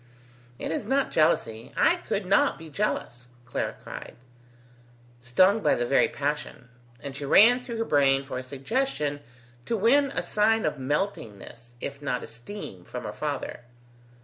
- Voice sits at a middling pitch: Yes, medium, 145 Hz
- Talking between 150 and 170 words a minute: Yes, average, 155 wpm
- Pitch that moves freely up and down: Yes, wide, 8.9 semitones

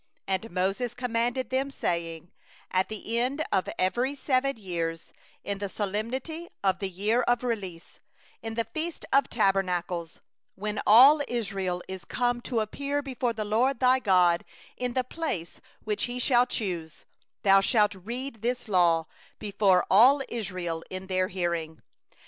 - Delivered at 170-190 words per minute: No, average, 150 wpm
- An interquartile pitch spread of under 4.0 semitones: No, average, 5.0 semitones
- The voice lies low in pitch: No, high, 215 Hz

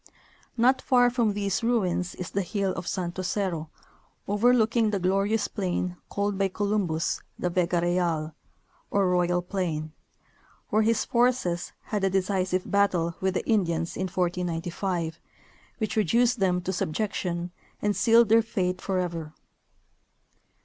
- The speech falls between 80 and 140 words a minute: Yes, slow, 135 wpm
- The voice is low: No, high, 190 Hz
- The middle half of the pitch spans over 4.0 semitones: No, average, 3.2 semitones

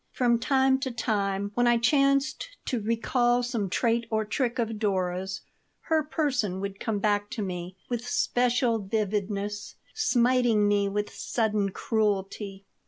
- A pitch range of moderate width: Yes, average, 3.4 semitones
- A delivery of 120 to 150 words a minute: Yes, average, 140 wpm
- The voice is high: Yes, high, 220 Hz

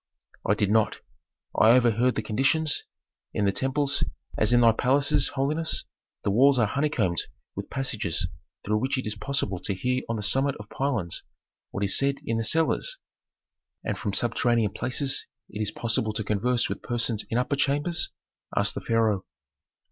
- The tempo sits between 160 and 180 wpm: Yes, average, 170 wpm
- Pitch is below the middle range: Yes, low, 120 Hz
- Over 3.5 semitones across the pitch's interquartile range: Yes, average, 4.4 semitones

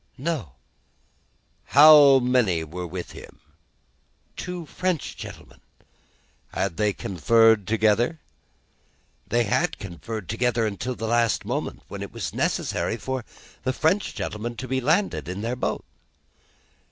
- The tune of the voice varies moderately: Yes, average, 4.2 semitones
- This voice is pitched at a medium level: No, low, 120 Hz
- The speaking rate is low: Yes, slow, 125 wpm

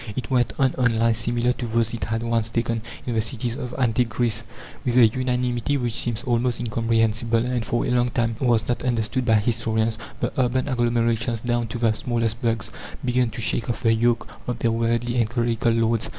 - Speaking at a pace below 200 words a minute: No, fast, 205 wpm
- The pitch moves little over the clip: Yes, narrow, 1.3 semitones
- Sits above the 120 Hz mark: No, low, 115 Hz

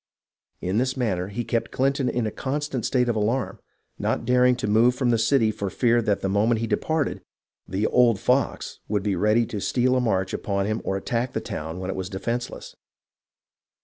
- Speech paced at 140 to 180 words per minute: No, average, 200 wpm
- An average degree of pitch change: Yes, average, 3.5 semitones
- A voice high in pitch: No, low, 115 Hz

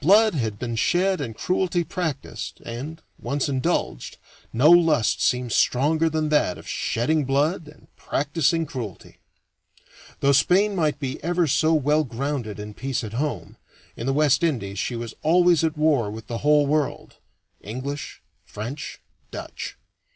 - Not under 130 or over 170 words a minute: Yes, average, 150 wpm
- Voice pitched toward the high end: No, medium, 145 Hz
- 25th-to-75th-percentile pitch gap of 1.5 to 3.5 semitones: No, average, 4.9 semitones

